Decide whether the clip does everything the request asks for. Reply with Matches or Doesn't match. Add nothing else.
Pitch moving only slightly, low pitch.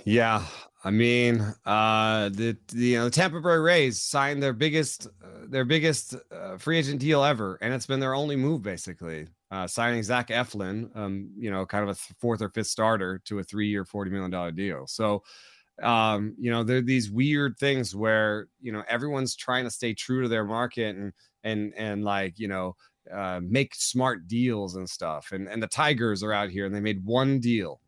Doesn't match